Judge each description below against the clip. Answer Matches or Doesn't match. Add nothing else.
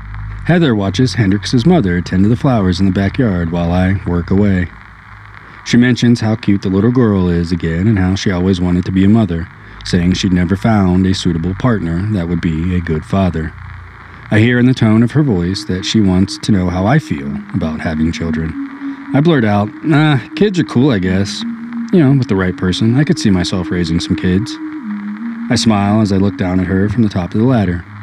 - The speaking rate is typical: Doesn't match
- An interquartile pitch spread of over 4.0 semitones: Matches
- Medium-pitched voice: Doesn't match